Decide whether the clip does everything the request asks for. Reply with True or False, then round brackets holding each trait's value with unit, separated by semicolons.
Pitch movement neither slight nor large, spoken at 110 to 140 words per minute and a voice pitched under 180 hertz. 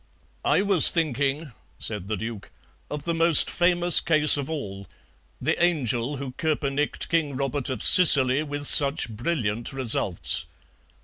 True (4.8 semitones; 135 wpm; 140 Hz)